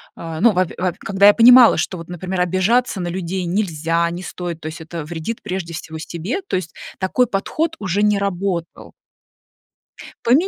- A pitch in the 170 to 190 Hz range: Yes, medium, 185 Hz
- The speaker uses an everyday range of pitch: Yes, average, 3.3 semitones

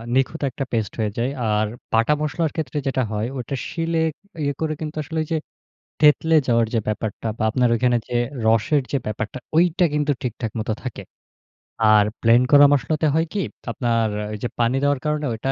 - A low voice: Yes, low, 130 Hz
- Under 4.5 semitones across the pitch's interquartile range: No, average, 4.9 semitones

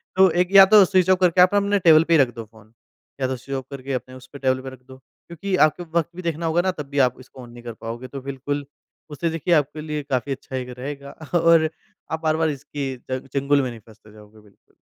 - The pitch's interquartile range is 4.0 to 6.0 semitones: Yes, average, 4.3 semitones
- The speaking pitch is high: No, medium, 140 Hz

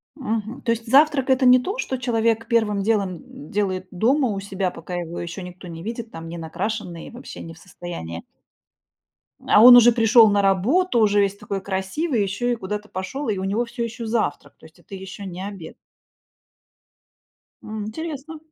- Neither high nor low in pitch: No, high, 210 Hz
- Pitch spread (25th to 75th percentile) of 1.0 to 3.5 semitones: No, average, 4.2 semitones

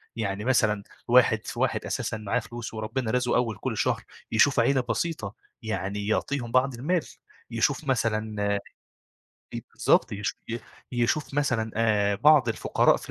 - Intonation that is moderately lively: Yes, average, 3.2 semitones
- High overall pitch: No, low, 115 Hz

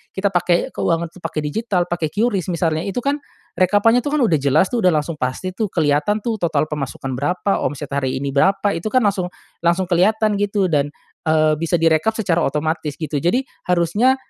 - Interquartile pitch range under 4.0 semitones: No, average, 4.8 semitones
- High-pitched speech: No, medium, 175 Hz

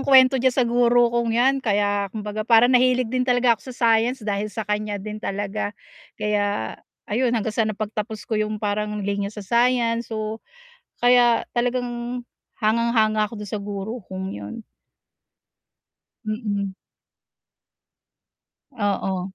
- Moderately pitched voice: No, high, 220 Hz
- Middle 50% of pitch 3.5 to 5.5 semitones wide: No, average, 2.7 semitones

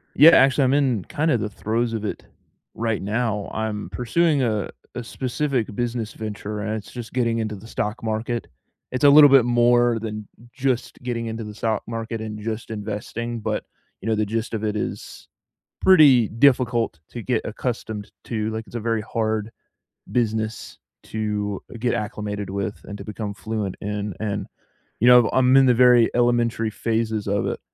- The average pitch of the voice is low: Yes, low, 115 Hz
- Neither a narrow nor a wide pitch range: No, narrow, 2.3 semitones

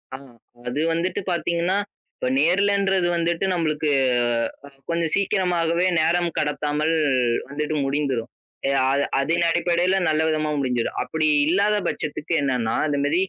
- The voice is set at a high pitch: No, medium, 165 Hz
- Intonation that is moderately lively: Yes, average, 3.1 semitones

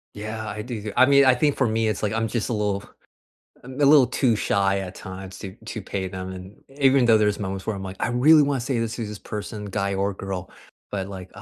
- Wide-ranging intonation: No, average, 3.8 semitones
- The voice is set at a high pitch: No, low, 105 Hz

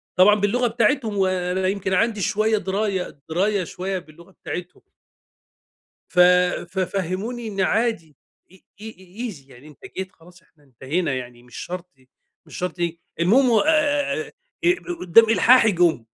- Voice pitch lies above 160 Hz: Yes, high, 190 Hz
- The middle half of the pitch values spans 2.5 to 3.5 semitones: No, average, 4.2 semitones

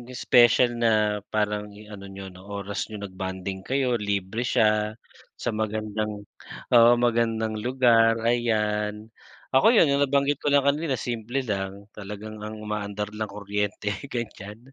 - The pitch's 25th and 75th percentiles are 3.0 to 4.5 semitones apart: No, narrow, 2.5 semitones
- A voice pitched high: No, low, 110 Hz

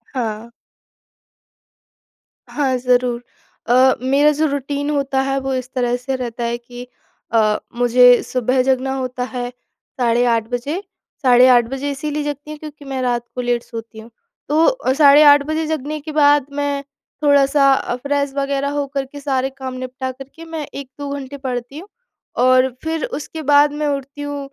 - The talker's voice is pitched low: No, very high, 270 Hz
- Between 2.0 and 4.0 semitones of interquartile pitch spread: Yes, narrow, 2.4 semitones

